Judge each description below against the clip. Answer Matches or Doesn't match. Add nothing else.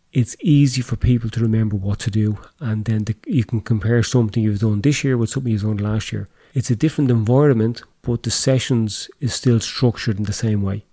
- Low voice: Matches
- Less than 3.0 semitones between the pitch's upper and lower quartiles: Matches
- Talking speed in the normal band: Doesn't match